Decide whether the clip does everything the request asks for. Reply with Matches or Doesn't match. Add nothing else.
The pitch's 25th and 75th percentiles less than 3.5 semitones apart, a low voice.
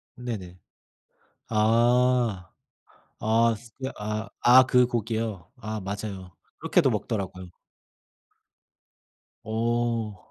Matches